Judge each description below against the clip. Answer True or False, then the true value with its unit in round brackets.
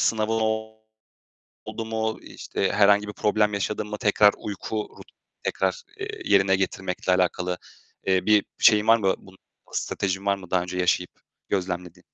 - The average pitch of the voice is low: True (100 Hz)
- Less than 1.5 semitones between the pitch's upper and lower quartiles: False (2.5 semitones)